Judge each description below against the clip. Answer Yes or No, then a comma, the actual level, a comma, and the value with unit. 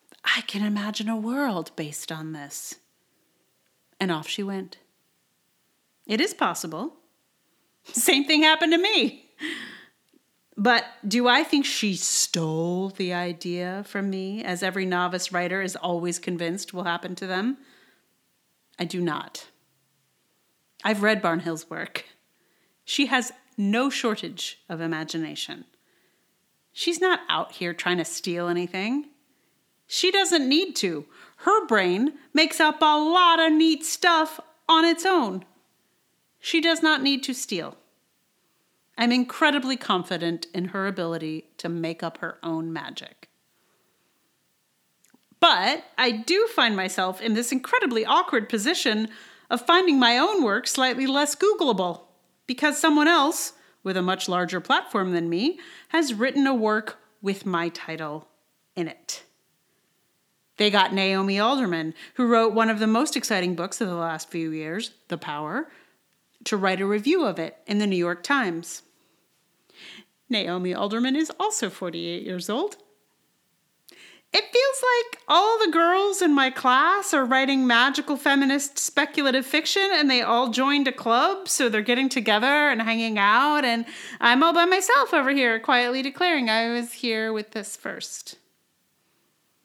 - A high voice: Yes, high, 235 Hz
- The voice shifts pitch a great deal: Yes, wide, 8.6 semitones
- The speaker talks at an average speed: Yes, average, 145 wpm